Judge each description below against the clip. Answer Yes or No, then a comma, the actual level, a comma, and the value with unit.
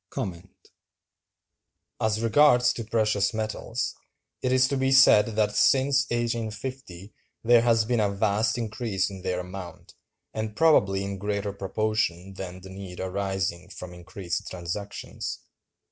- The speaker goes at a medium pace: No, slow, 130 wpm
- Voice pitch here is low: Yes, low, 105 Hz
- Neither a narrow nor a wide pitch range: Yes, average, 3.3 semitones